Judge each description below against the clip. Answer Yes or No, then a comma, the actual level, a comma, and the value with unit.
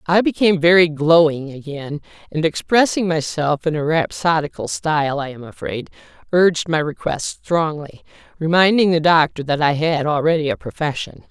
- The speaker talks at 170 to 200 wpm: No, average, 150 wpm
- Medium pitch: Yes, medium, 160 Hz